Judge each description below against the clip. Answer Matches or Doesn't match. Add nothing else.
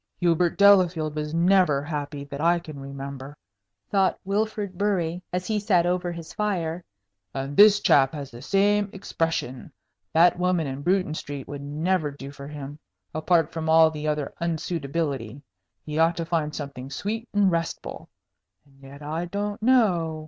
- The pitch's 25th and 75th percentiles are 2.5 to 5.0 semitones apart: Matches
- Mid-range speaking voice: Matches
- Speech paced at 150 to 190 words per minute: Matches